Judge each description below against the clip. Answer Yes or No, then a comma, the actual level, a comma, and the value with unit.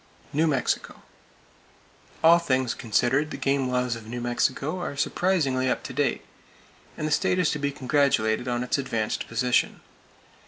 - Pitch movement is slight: No, average, 3.2 semitones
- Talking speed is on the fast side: No, average, 155 wpm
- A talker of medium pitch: No, low, 130 Hz